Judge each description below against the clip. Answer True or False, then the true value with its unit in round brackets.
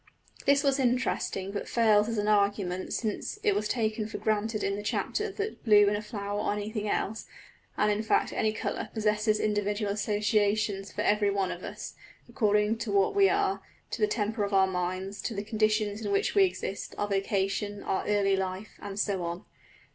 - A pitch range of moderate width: False (1.4 semitones)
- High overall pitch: True (210 Hz)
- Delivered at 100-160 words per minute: False (195 wpm)